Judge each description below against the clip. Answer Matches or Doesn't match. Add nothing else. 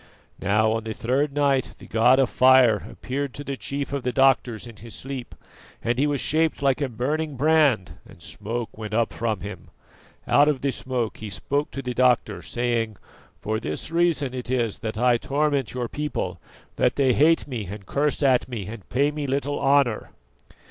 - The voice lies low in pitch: Matches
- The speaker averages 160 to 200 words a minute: Matches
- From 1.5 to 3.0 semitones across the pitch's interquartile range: Doesn't match